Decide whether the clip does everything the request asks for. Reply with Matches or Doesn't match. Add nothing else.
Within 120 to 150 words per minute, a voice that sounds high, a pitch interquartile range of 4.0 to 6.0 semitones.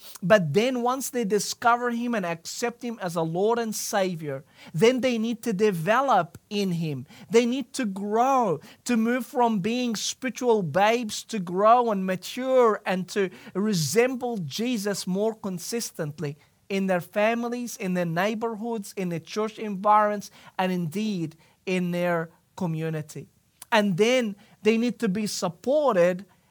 Matches